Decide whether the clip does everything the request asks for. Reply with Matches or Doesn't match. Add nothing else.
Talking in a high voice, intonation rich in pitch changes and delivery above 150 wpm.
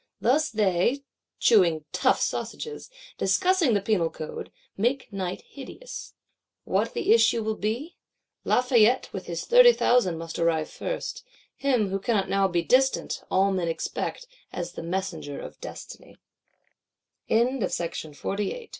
Doesn't match